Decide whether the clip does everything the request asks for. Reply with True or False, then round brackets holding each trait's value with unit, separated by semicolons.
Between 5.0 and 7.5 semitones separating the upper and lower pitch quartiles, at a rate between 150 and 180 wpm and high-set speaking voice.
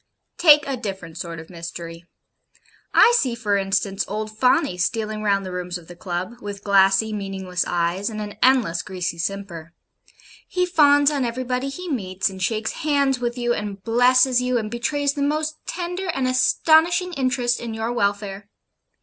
True (5.3 semitones; 165 wpm; 220 Hz)